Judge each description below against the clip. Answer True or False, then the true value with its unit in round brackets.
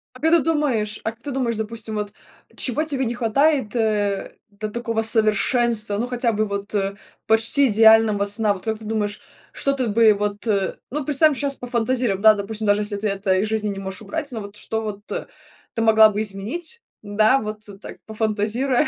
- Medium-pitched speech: False (220 Hz)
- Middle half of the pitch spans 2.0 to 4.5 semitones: True (2.9 semitones)